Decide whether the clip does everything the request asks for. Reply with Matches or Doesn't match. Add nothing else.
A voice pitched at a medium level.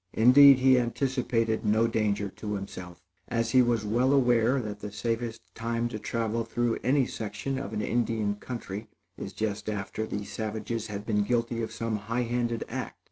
Doesn't match